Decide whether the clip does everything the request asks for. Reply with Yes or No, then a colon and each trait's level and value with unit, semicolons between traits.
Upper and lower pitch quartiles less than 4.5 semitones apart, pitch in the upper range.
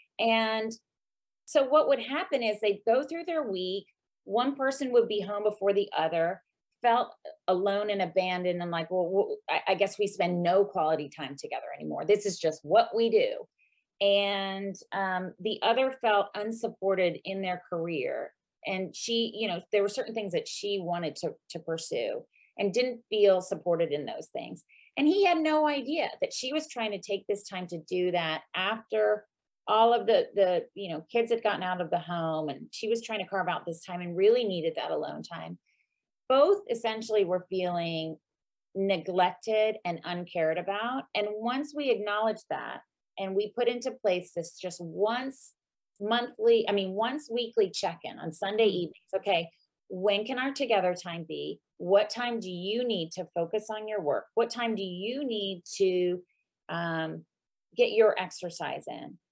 No: average, 4.8 semitones; high, 205 Hz